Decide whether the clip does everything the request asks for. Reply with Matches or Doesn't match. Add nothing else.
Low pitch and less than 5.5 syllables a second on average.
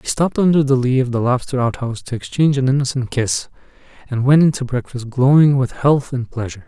Doesn't match